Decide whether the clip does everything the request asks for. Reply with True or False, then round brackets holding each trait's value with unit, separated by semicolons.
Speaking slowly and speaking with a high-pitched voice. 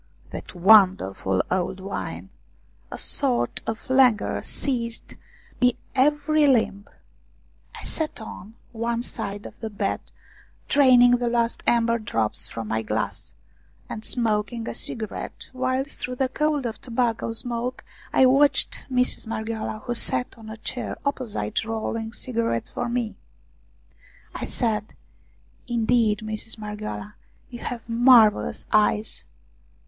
True (125 wpm; 230 Hz)